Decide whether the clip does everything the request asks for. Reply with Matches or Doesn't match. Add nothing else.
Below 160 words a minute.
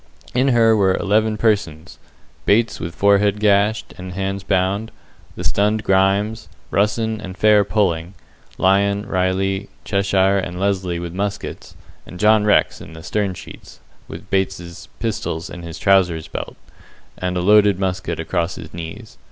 Matches